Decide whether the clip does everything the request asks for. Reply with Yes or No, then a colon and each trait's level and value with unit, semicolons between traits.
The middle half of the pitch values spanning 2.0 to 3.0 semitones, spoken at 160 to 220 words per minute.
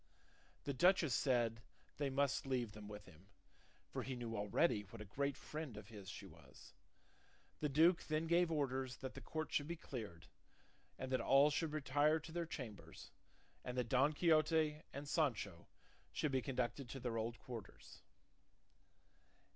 No: average, 5.0 semitones; average, 165 wpm